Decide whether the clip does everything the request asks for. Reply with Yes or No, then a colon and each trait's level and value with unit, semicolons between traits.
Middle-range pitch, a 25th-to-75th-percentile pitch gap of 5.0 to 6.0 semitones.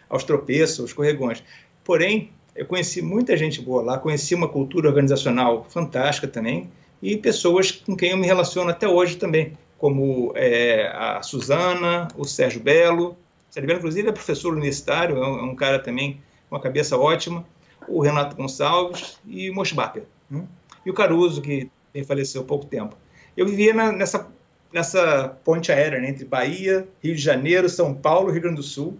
No: medium, 160 Hz; average, 4.3 semitones